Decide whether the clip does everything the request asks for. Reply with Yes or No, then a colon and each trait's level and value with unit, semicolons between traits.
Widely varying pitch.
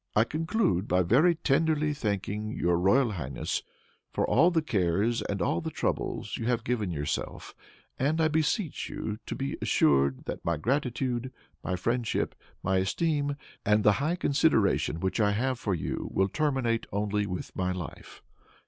Yes: wide, 7.2 semitones